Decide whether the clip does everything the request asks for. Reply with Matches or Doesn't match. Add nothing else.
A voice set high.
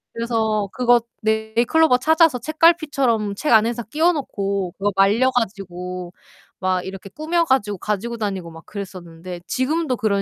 Matches